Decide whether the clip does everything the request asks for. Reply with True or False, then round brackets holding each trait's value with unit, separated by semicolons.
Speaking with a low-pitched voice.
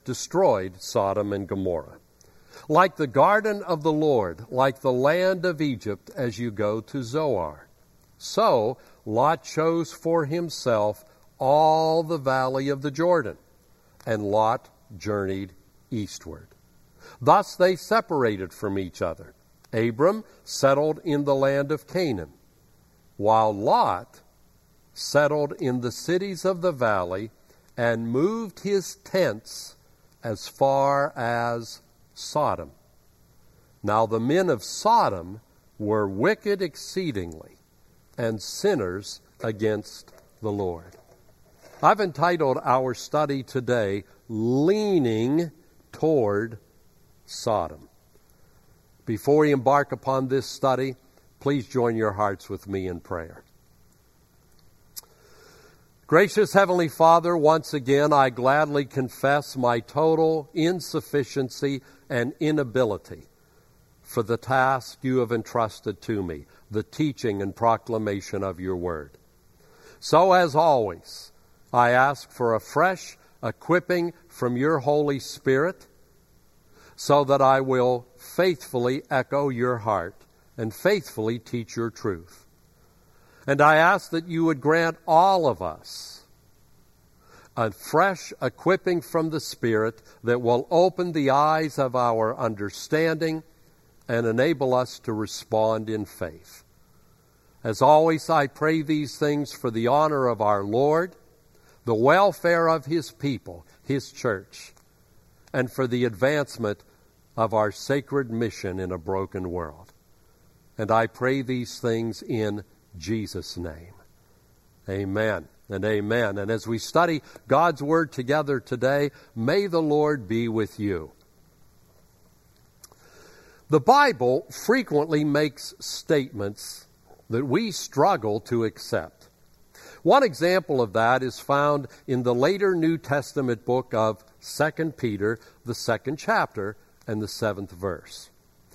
True (130 Hz)